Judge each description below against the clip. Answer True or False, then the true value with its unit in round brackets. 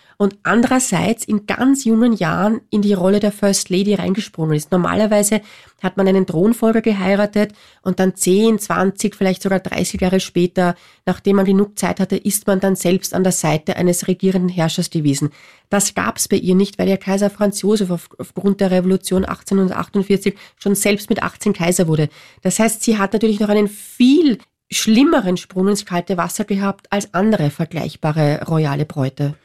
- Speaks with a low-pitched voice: False (195 Hz)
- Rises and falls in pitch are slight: True (2.3 semitones)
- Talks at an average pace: True (175 wpm)